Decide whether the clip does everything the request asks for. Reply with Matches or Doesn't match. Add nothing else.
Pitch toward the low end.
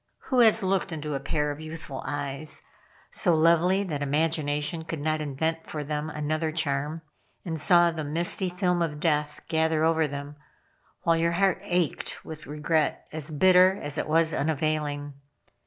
Doesn't match